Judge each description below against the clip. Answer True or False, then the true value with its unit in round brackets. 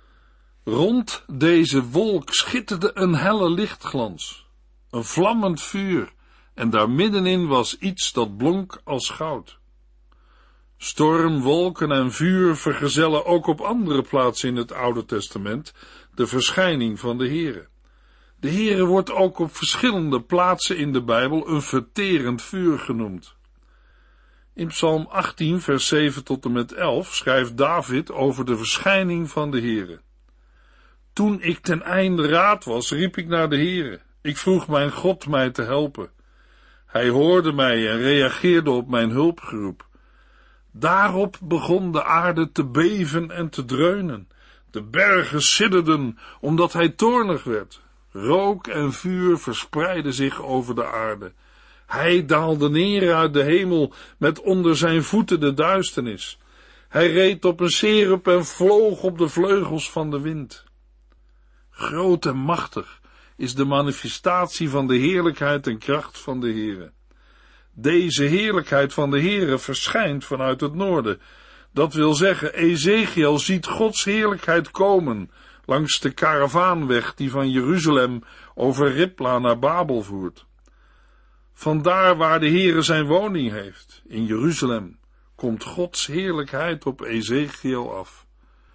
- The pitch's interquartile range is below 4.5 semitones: False (5.5 semitones)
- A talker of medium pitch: True (155 Hz)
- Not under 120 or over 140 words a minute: True (135 wpm)